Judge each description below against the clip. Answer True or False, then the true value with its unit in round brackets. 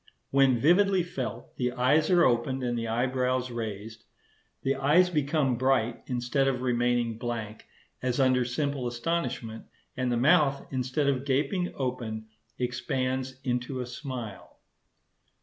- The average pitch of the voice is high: False (130 Hz)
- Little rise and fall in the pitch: True (2.3 semitones)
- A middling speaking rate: False (130 wpm)